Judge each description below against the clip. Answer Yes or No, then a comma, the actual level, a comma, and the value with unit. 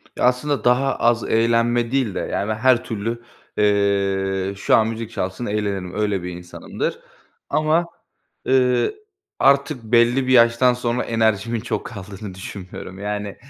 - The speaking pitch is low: Yes, low, 115 Hz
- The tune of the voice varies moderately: Yes, average, 3.4 semitones